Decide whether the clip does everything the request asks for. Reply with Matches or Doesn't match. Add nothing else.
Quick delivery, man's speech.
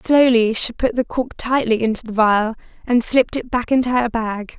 Doesn't match